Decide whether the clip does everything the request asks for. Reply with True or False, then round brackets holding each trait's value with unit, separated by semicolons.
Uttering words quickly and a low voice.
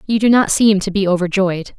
False (235 wpm; 195 Hz)